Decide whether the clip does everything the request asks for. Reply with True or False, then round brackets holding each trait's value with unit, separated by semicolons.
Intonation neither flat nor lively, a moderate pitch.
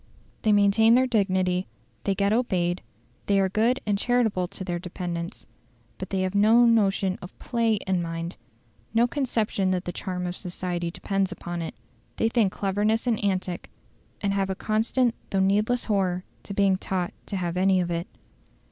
False (3.1 semitones; 195 Hz)